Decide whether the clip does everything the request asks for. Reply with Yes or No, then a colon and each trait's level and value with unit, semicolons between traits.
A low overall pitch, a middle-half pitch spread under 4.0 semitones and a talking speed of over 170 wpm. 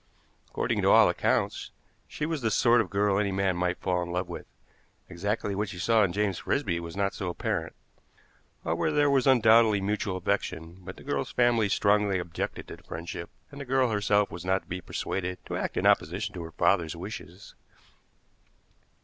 Yes: low, 100 Hz; average, 3.6 semitones; average, 190 wpm